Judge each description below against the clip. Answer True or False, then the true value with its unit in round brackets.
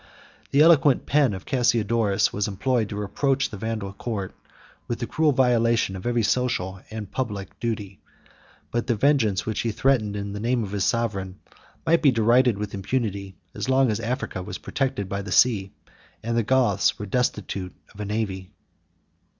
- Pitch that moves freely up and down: False (3.9 semitones)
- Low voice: True (110 Hz)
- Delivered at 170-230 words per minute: True (175 wpm)